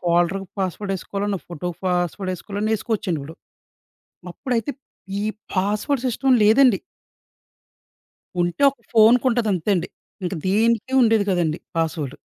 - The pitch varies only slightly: No, average, 4.3 semitones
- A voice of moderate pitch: No, high, 200 Hz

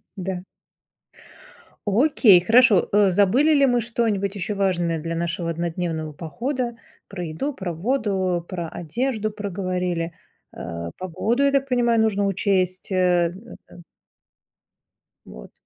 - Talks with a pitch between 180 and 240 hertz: Yes, high, 190 Hz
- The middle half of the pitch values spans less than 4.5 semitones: No, average, 5.0 semitones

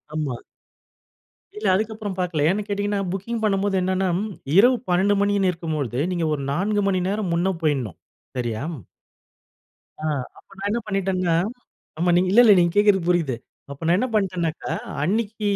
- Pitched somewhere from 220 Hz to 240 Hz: No, high, 190 Hz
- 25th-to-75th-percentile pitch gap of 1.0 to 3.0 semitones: No, average, 3.4 semitones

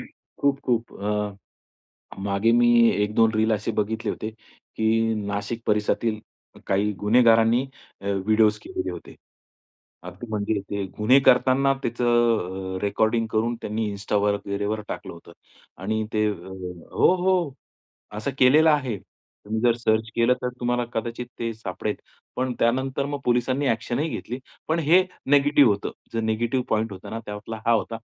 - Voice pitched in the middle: No, low, 115 Hz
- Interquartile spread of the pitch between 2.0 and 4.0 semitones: Yes, average, 2.8 semitones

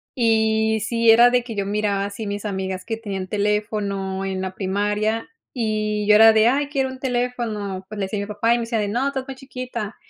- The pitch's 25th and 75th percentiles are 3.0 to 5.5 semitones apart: No, narrow, 2.6 semitones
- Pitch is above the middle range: Yes, high, 215 Hz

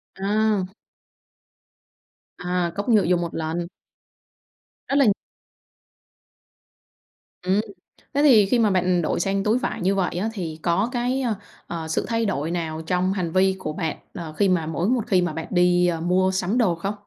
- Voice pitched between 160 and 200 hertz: Yes, medium, 185 Hz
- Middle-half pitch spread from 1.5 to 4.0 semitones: Yes, average, 3.4 semitones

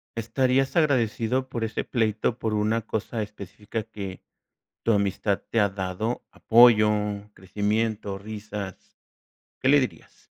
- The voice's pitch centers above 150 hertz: No, low, 110 Hz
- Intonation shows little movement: Yes, narrow, 2.2 semitones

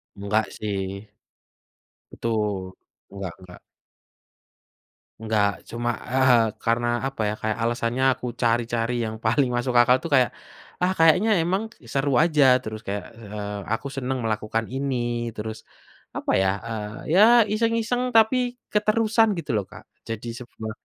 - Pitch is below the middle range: Yes, low, 120 Hz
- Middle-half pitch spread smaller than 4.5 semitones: No, wide, 5.4 semitones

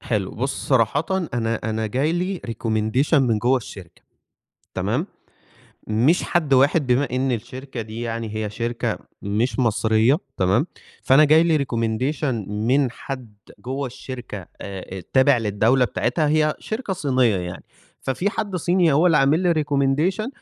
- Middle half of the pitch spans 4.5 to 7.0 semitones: Yes, average, 5.1 semitones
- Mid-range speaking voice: No, low, 130 Hz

